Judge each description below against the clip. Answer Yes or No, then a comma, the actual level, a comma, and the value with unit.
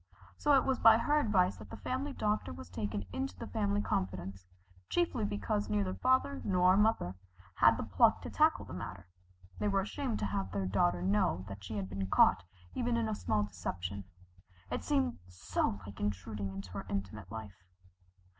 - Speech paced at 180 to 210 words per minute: Yes, average, 185 wpm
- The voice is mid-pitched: No, low, 100 Hz